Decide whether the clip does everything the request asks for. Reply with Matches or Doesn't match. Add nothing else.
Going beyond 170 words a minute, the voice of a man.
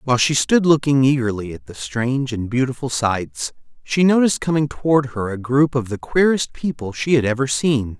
Matches